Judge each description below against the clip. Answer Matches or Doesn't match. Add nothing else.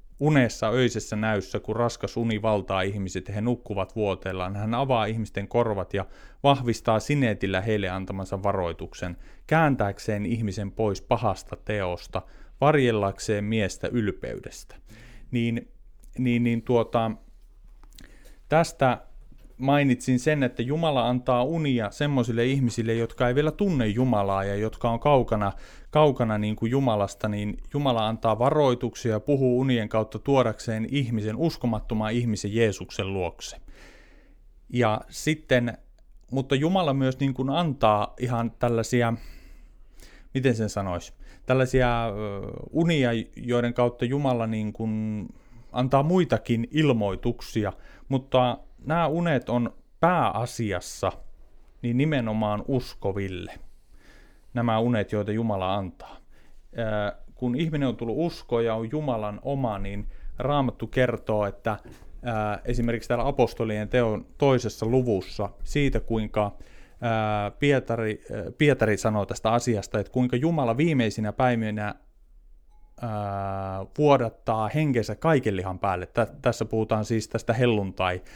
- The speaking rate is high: Doesn't match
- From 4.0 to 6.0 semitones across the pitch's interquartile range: Doesn't match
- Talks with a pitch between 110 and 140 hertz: Matches